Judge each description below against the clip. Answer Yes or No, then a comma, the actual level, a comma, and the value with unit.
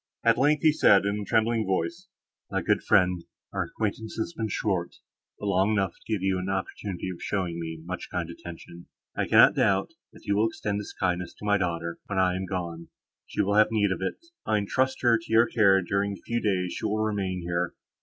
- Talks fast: Yes, fast, 220 wpm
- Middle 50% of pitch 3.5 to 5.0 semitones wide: No, average, 3.1 semitones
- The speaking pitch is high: No, low, 100 Hz